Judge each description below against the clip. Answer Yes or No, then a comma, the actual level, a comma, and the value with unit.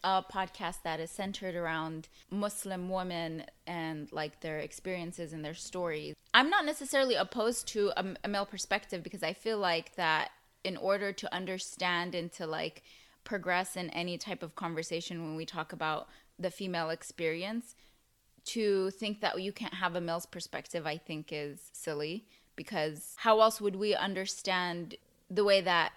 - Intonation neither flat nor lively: Yes, average, 3.3 semitones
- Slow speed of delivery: No, average, 165 wpm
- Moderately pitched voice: Yes, medium, 180 Hz